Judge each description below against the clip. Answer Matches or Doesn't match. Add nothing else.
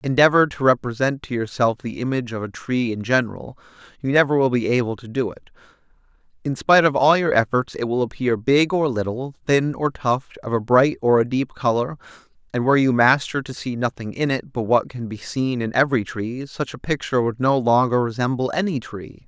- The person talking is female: Doesn't match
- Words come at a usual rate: Doesn't match